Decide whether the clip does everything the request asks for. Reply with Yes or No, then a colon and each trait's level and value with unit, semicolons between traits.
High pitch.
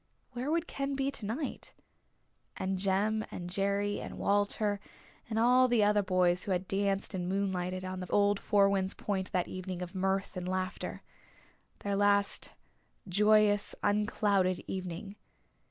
Yes: high, 200 Hz